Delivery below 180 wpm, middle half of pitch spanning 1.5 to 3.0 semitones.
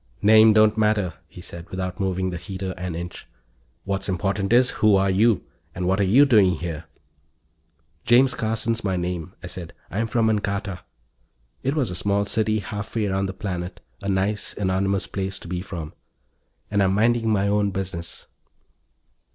Yes: average, 170 wpm; average, 2.7 semitones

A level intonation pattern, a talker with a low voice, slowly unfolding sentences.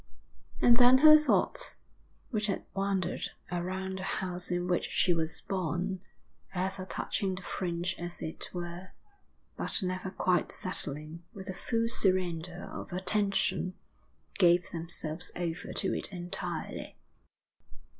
No: narrow, 1.8 semitones; medium, 185 Hz; slow, 125 wpm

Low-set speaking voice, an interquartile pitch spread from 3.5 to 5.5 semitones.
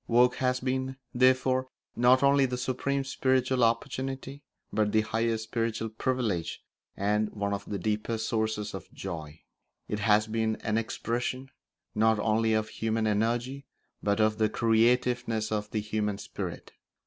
No: low, 115 Hz; average, 3.0 semitones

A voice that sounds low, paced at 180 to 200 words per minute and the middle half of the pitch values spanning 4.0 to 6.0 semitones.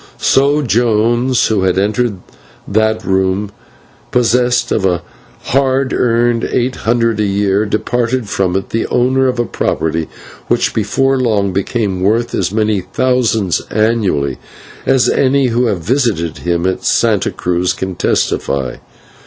No: low, 110 Hz; slow, 135 wpm; average, 4.4 semitones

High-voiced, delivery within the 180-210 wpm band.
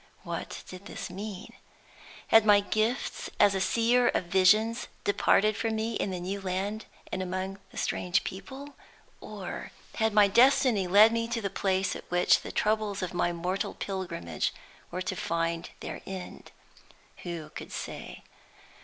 No: high, 195 Hz; average, 155 wpm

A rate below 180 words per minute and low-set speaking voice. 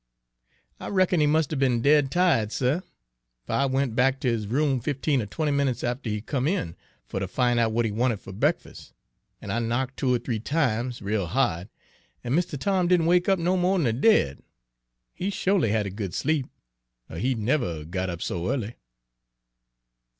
No: average, 200 wpm; low, 130 Hz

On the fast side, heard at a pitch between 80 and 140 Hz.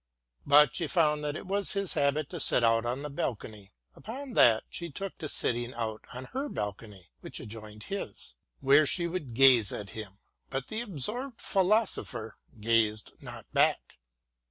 No: average, 180 wpm; low, 135 Hz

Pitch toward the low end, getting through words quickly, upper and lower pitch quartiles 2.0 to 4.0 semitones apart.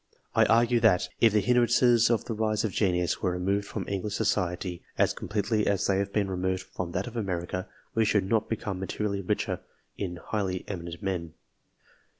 No: low, 100 Hz; average, 185 wpm; average, 3.2 semitones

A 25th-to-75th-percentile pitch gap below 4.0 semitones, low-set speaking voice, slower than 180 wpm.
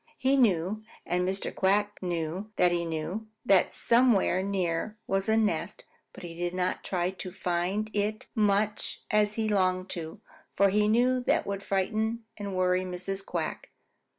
No: average, 2.8 semitones; high, 195 Hz; average, 160 wpm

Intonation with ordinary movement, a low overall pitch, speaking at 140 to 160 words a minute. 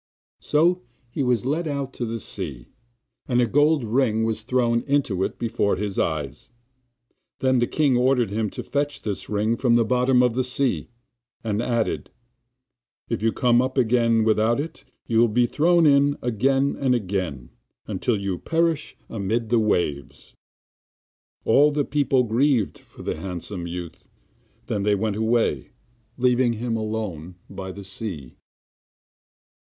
Yes: average, 4.1 semitones; low, 115 Hz; average, 155 wpm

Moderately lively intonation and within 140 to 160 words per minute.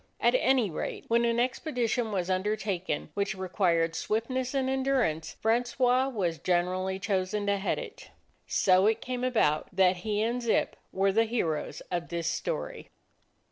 Yes: average, 4.9 semitones; average, 155 wpm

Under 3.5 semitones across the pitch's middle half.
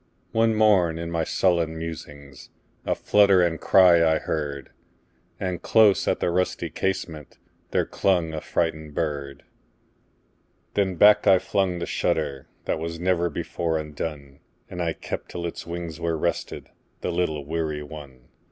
Yes: average, 2.8 semitones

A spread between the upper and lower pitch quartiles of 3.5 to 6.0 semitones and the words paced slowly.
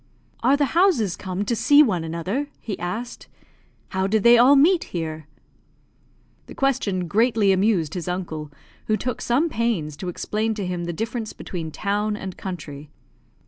No: average, 5.1 semitones; average, 160 wpm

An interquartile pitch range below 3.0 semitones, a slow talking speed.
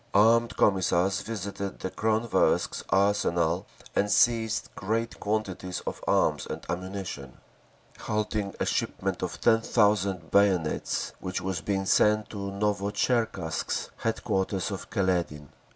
Yes: narrow, 2.5 semitones; slow, 115 wpm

